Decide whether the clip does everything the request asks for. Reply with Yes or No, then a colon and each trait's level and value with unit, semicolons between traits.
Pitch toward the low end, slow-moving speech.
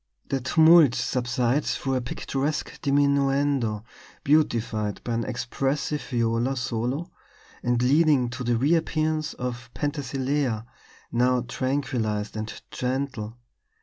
Yes: low, 130 Hz; slow, 105 wpm